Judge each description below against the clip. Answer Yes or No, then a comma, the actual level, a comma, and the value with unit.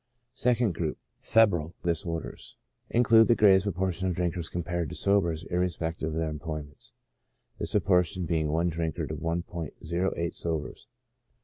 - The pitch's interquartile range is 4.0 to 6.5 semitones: No, narrow, 2.5 semitones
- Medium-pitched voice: No, very low, 85 Hz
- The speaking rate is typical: No, slow, 130 wpm